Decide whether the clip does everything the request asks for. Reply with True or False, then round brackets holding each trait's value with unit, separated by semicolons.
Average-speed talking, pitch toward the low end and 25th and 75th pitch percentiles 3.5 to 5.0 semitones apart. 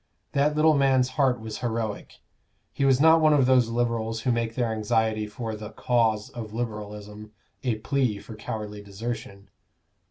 False (160 wpm; 115 Hz; 3.1 semitones)